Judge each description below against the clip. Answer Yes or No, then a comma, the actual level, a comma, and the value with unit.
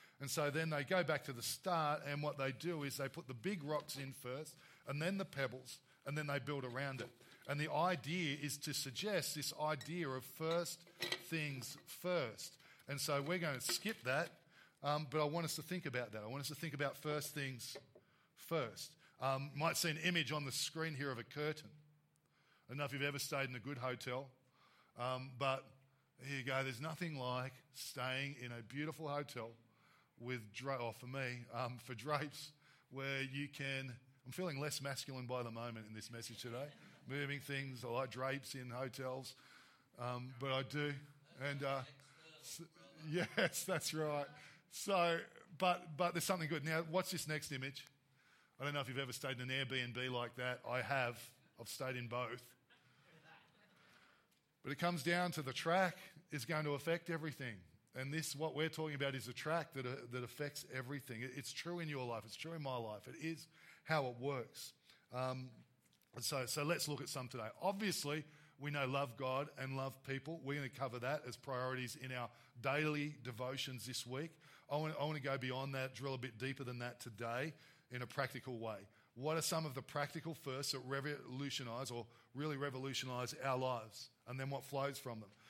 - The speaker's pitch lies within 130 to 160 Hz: Yes, medium, 140 Hz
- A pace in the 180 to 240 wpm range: Yes, average, 195 wpm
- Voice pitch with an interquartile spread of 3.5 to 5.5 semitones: No, average, 3.0 semitones